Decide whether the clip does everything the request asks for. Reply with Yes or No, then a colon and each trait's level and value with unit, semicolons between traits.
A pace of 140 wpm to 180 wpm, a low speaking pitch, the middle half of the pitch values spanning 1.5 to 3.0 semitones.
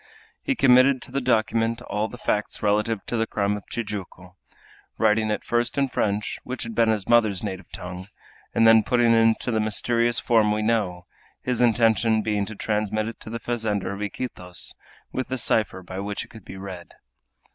No: average, 190 wpm; low, 110 Hz; narrow, 2.4 semitones